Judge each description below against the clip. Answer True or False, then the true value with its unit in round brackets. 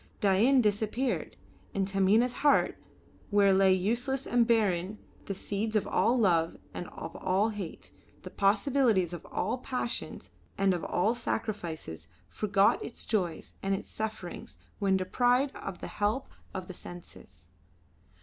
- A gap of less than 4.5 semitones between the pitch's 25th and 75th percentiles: True (3.8 semitones)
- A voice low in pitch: False (200 Hz)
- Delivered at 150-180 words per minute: False (140 wpm)